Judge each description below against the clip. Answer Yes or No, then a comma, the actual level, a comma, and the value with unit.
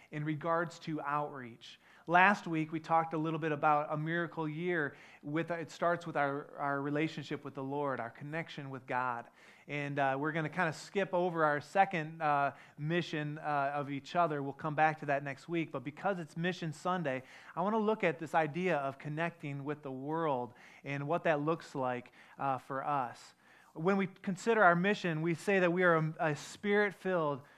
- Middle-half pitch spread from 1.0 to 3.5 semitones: Yes, average, 3.1 semitones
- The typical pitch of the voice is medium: Yes, medium, 155 Hz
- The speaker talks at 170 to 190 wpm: No, average, 200 wpm